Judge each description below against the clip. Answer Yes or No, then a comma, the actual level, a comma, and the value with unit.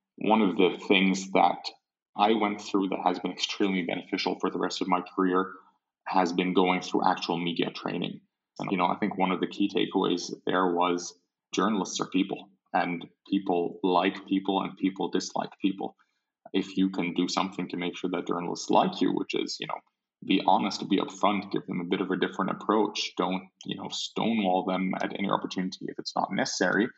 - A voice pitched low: Yes, very low, 95 Hz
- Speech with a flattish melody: Yes, narrow, 1.1 semitones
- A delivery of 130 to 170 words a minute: No, average, 200 wpm